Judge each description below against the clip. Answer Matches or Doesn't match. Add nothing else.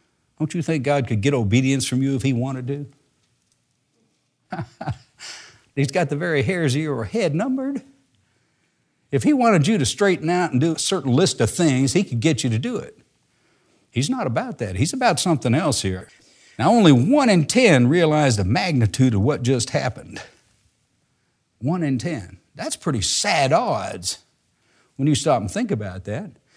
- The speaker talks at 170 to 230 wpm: Matches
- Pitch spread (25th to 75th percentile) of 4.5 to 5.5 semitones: Matches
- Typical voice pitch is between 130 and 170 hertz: Matches